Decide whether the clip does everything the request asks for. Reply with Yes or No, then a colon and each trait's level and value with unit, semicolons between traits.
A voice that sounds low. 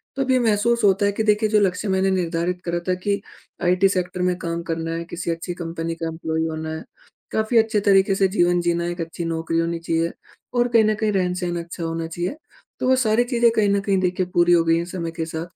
No: medium, 180 Hz